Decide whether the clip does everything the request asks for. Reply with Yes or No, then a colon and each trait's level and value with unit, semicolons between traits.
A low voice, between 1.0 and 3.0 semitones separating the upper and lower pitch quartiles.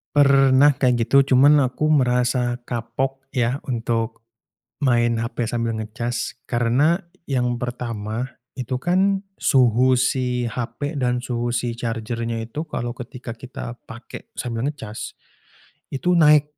Yes: low, 125 Hz; narrow, 2.5 semitones